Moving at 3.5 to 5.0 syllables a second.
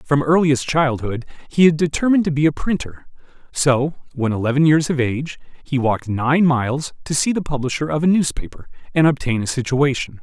No: 5.7 syllables/s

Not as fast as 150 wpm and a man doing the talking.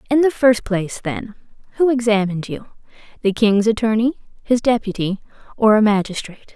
No: slow, 135 wpm; female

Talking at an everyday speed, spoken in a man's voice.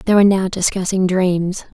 No: average, 165 wpm; female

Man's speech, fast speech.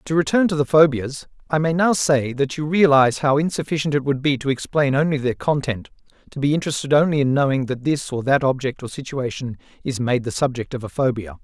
Yes: male; fast, 220 wpm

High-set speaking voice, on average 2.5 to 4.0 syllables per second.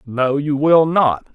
No: medium, 145 Hz; 3.4 syllables/s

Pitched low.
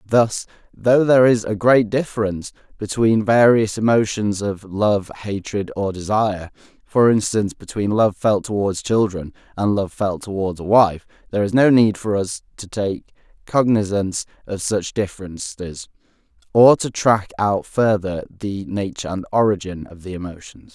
Yes: low, 105 Hz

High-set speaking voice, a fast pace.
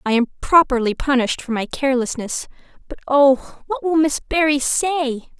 No: very high, 275 Hz; average, 155 wpm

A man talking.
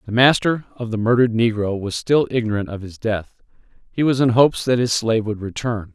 Yes: male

